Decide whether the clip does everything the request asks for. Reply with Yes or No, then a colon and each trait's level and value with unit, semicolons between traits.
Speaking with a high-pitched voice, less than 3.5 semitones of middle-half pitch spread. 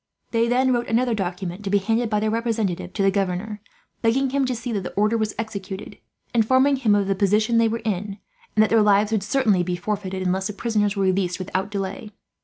Yes: high, 210 Hz; average, 2.8 semitones